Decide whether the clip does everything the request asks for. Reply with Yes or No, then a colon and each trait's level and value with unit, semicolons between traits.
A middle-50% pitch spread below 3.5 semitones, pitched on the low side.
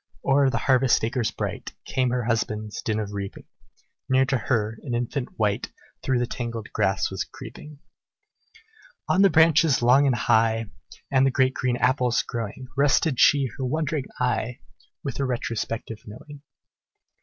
Yes: average, 3.1 semitones; low, 125 Hz